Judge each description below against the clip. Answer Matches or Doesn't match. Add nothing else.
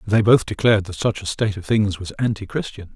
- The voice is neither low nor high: Doesn't match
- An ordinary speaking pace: Doesn't match